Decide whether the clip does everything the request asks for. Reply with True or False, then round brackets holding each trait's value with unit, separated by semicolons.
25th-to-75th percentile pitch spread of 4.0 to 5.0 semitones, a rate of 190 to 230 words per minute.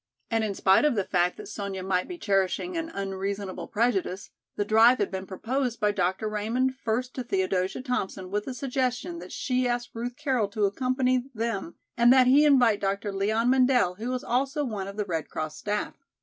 True (4.4 semitones; 195 wpm)